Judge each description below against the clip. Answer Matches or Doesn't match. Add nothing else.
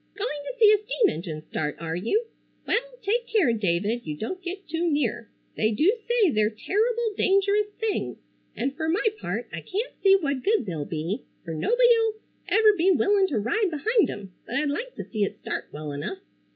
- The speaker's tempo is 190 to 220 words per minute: Matches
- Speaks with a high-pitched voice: Matches